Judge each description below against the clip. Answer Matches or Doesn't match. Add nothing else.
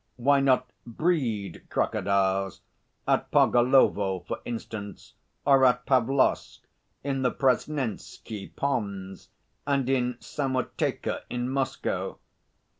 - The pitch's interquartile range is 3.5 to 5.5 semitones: Matches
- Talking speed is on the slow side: Matches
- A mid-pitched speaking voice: Doesn't match